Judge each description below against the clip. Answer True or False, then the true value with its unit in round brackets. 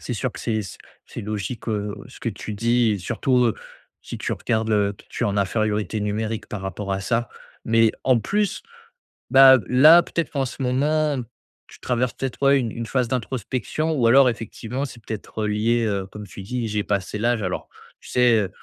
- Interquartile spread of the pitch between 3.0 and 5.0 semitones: True (3.3 semitones)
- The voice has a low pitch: True (115 Hz)